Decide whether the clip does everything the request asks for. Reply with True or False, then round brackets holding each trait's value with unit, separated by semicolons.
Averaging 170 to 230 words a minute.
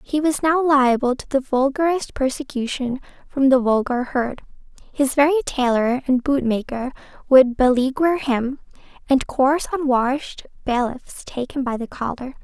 False (140 wpm)